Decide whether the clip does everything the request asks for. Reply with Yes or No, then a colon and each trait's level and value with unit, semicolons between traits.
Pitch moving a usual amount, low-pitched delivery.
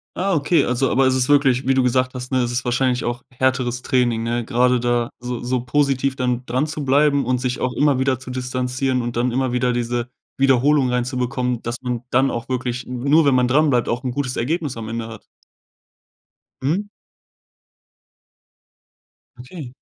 No: narrow, 1.6 semitones; low, 125 Hz